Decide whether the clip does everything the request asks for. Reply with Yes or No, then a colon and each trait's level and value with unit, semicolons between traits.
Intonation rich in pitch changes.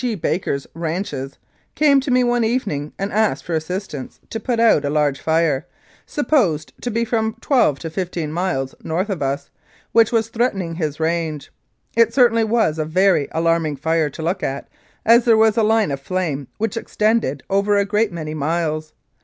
Yes: wide, 6.5 semitones